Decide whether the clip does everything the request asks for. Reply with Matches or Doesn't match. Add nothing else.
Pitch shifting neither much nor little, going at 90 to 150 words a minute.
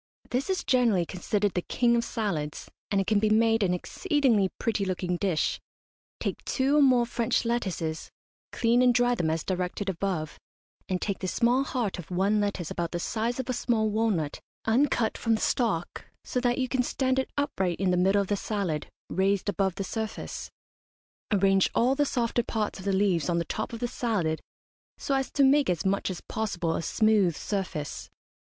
Doesn't match